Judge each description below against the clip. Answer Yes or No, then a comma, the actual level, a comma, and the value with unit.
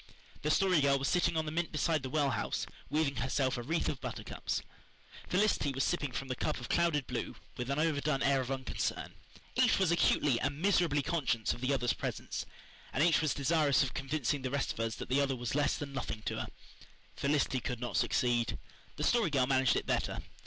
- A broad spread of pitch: No, average, 3.1 semitones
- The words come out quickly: Yes, fast, 210 wpm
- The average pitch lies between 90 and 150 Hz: Yes, medium, 140 Hz